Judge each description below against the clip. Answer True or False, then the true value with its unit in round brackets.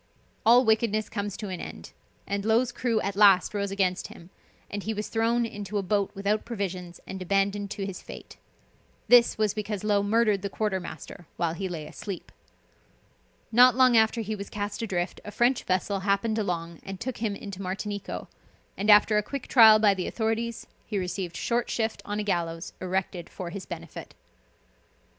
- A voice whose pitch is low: False (205 Hz)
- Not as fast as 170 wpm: False (180 wpm)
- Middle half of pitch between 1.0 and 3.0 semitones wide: True (2.5 semitones)